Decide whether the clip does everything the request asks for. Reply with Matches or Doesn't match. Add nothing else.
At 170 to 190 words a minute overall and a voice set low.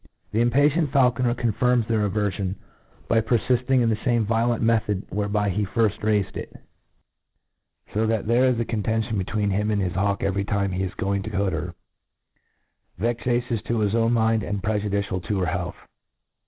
Matches